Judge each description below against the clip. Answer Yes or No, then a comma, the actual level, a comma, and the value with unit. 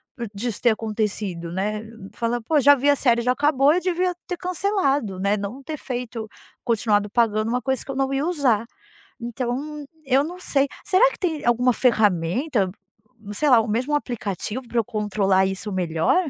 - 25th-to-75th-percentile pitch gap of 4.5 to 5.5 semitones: Yes, average, 5.2 semitones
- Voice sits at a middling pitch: No, high, 240 Hz